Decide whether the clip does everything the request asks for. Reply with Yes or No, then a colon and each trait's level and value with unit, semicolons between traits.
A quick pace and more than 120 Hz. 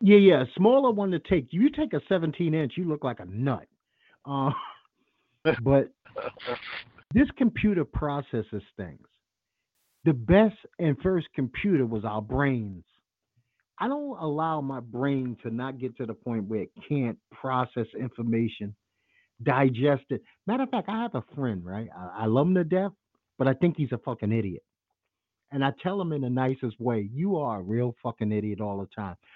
No: average, 175 wpm; low, 135 Hz